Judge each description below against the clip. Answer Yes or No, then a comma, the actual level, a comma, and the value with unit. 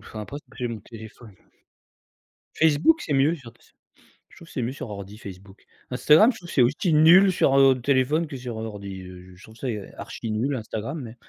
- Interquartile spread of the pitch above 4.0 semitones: Yes, wide, 5.5 semitones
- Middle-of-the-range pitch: No, low, 120 Hz